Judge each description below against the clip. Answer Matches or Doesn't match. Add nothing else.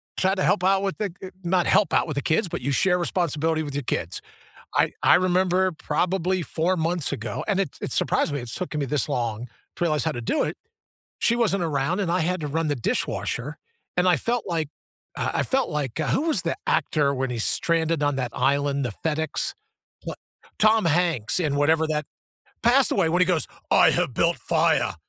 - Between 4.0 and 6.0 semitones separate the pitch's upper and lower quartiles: Matches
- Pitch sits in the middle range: Matches